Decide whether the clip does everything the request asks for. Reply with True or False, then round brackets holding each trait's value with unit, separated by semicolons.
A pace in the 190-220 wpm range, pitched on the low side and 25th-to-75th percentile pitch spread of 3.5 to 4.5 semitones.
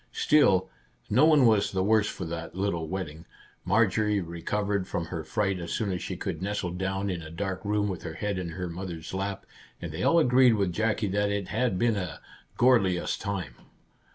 False (195 wpm; 95 Hz; 3.0 semitones)